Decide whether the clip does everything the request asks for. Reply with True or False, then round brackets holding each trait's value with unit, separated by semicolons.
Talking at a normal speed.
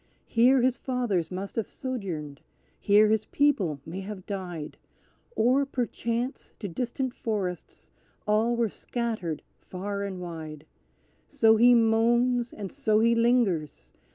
False (125 wpm)